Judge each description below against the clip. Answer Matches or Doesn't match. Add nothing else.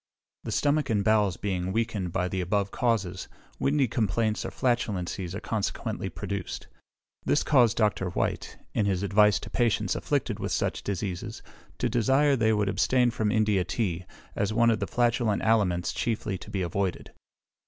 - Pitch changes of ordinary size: Matches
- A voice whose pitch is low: Matches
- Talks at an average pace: Matches